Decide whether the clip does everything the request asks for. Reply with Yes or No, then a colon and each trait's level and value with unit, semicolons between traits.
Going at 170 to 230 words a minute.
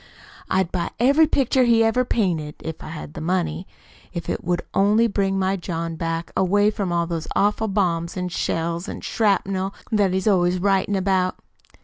Yes: average, 175 wpm